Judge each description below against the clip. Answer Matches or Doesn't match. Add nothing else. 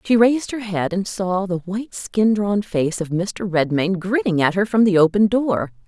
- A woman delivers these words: Matches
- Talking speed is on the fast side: Matches